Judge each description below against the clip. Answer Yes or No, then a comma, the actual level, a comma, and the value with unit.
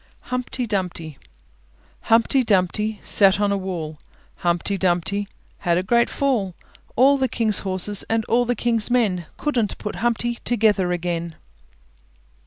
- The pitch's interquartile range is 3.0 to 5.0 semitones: Yes, average, 4.7 semitones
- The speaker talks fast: No, average, 140 wpm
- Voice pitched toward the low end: No, high, 205 Hz